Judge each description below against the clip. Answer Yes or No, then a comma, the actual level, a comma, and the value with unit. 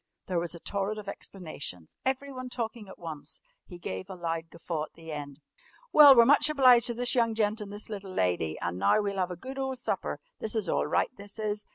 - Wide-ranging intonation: Yes, wide, 6.2 semitones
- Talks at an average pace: No, fast, 225 wpm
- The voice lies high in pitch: Yes, high, 200 Hz